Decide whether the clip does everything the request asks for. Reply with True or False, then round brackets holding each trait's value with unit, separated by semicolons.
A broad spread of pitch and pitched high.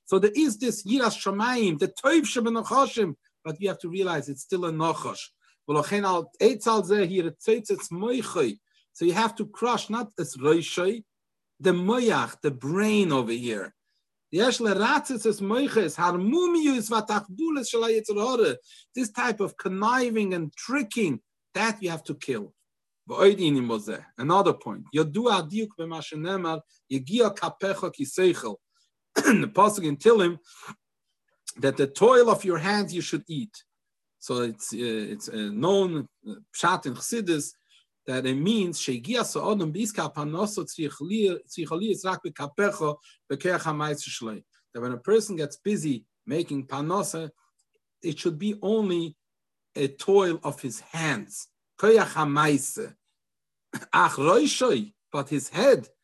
True (6.2 semitones; 195 Hz)